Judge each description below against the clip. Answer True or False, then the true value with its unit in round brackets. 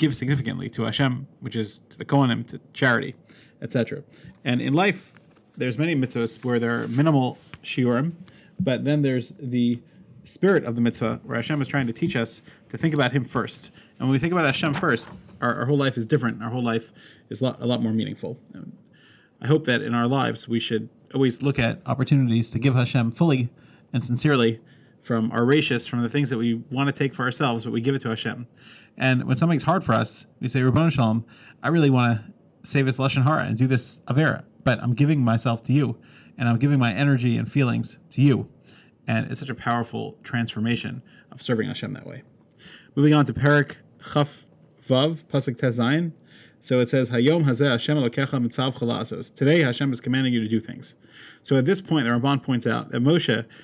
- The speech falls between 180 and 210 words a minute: True (205 wpm)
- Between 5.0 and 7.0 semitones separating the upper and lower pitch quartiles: False (3.4 semitones)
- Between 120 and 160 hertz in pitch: True (130 Hz)